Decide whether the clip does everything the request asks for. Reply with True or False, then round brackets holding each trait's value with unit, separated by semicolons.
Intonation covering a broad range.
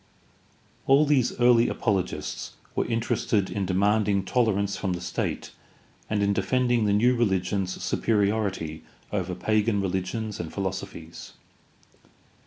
False (3.2 semitones)